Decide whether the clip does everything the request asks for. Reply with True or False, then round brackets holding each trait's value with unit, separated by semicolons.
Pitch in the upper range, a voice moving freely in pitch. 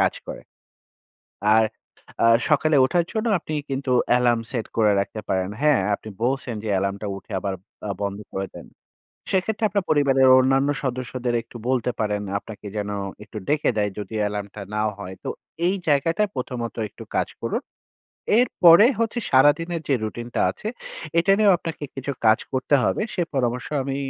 False (130 Hz; 6.1 semitones)